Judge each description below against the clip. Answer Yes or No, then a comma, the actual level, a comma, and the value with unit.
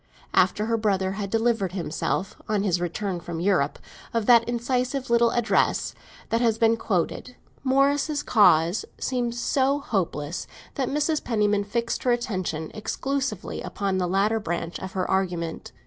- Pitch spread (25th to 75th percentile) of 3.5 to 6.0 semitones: Yes, average, 4.4 semitones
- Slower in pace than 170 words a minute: Yes, average, 145 wpm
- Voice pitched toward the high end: Yes, high, 215 Hz